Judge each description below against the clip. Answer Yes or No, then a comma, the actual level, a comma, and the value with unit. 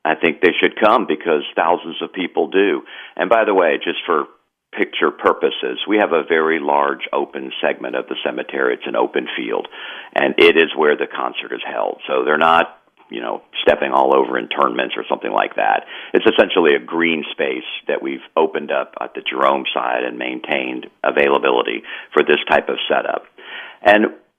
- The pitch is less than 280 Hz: No, very high, 380 Hz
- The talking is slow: No, average, 195 wpm